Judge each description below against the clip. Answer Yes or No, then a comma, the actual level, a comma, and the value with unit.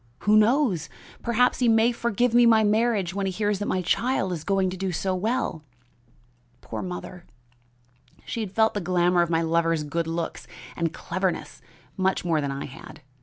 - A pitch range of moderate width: Yes, average, 4.5 semitones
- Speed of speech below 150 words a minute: No, average, 180 wpm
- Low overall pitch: No, high, 190 Hz